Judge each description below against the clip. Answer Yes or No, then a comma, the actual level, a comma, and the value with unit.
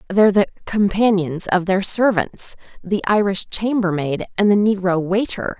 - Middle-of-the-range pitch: No, high, 195 Hz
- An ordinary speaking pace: No, slow, 130 wpm